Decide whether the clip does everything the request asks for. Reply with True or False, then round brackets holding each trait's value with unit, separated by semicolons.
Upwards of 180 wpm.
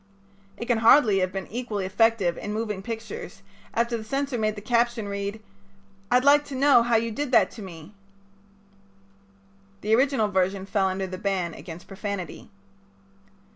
False (160 wpm)